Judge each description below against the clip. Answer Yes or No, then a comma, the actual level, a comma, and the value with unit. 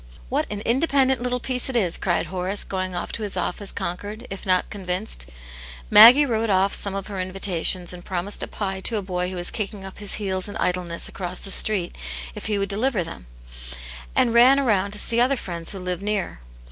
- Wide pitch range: No, average, 3.0 semitones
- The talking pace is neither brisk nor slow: No, fast, 210 wpm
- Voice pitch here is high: Yes, high, 195 Hz